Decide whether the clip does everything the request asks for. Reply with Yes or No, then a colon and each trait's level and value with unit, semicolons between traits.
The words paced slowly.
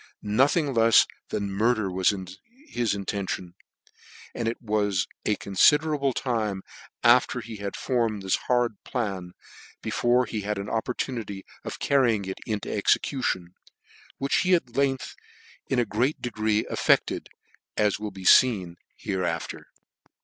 Yes: slow, 130 wpm